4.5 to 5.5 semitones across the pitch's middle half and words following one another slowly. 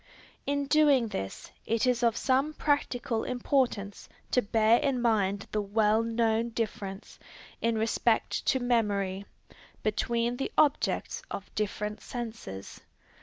No: average, 3.0 semitones; slow, 120 wpm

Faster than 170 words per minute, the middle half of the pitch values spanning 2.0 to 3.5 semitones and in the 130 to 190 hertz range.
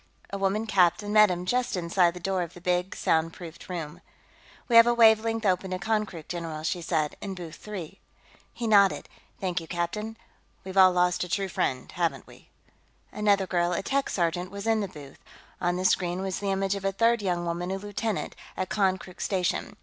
Yes: average, 195 wpm; average, 2.8 semitones; medium, 185 Hz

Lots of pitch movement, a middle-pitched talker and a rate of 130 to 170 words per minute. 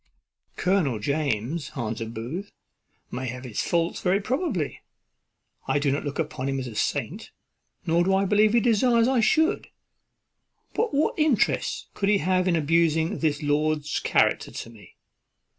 Yes: wide, 6.7 semitones; medium, 165 Hz; average, 155 wpm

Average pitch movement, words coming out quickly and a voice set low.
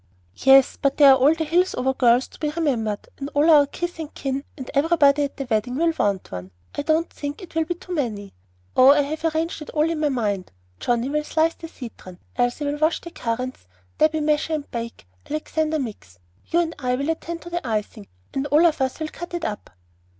No: average, 4.2 semitones; fast, 220 wpm; very high, 290 Hz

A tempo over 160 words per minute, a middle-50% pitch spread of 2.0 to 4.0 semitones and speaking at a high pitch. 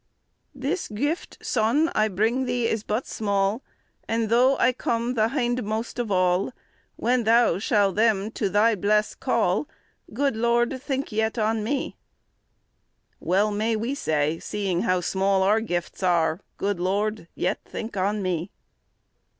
No: average, 145 wpm; average, 3.3 semitones; high, 215 Hz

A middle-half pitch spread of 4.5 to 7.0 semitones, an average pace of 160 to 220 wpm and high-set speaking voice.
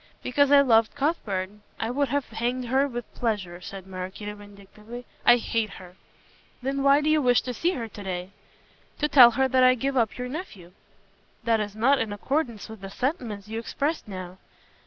Yes: average, 4.8 semitones; average, 190 wpm; high, 235 Hz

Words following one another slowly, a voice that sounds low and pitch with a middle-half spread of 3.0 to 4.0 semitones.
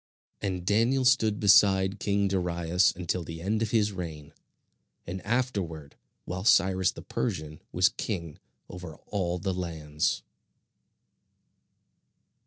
Yes: slow, 115 wpm; very low, 95 Hz; average, 3.3 semitones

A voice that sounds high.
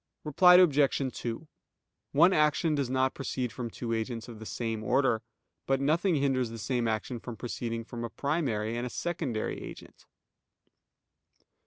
No: low, 130 Hz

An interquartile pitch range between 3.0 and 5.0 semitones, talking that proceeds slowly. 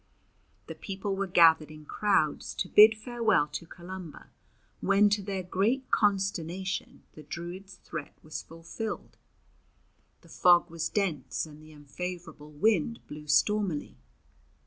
Yes: average, 4.4 semitones; slow, 125 wpm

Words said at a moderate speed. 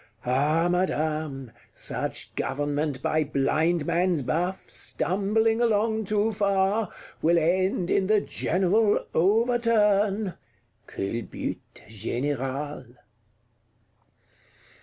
No: slow, 75 wpm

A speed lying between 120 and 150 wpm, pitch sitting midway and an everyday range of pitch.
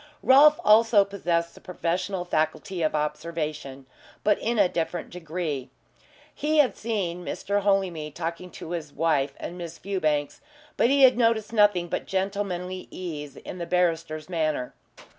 Yes: average, 145 wpm; medium, 175 Hz; average, 4.1 semitones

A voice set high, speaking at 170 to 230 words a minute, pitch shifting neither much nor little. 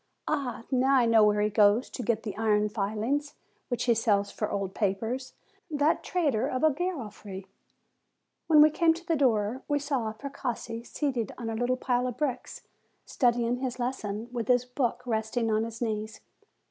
Yes: high, 240 Hz; average, 175 wpm; average, 3.6 semitones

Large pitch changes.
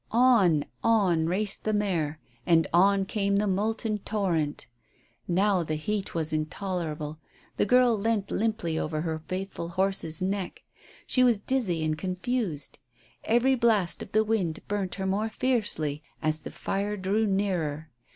No: average, 4.6 semitones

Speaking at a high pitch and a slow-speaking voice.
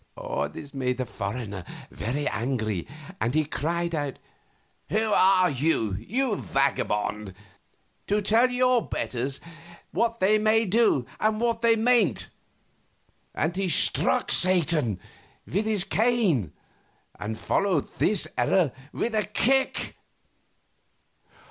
No: medium, 175 Hz; slow, 115 wpm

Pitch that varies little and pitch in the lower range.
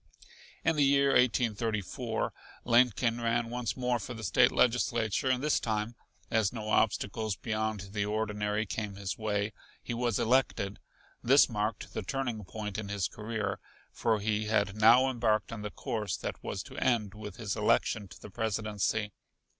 Yes: narrow, 2.3 semitones; low, 110 Hz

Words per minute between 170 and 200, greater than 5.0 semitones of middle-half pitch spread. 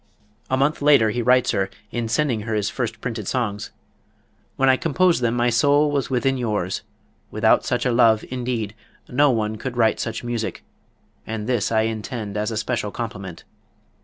No: average, 175 wpm; average, 2.7 semitones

